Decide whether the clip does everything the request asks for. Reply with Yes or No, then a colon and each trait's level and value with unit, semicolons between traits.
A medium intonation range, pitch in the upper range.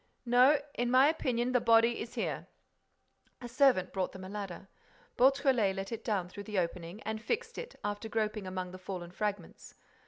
Yes: average, 4.5 semitones; high, 215 Hz